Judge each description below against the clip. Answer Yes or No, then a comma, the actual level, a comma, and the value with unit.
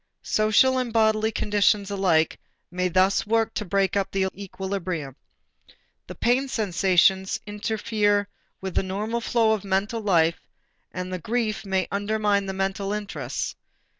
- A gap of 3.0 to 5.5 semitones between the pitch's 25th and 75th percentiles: No, narrow, 2.4 semitones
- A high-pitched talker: Yes, high, 200 Hz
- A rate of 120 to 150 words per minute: Yes, slow, 135 wpm